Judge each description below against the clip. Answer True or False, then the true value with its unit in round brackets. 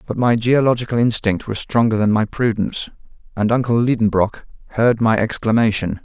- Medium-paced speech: True (150 wpm)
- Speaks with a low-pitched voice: True (110 Hz)